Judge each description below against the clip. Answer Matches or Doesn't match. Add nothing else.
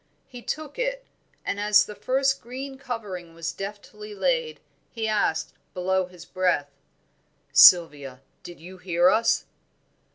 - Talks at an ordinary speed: Doesn't match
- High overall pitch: Matches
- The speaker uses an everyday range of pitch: Doesn't match